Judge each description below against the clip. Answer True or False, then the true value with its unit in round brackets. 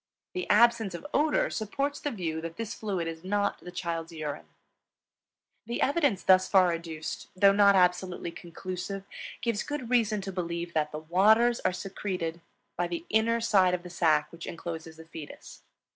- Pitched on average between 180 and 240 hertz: True (185 Hz)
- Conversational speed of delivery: True (170 wpm)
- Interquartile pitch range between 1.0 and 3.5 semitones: False (4.3 semitones)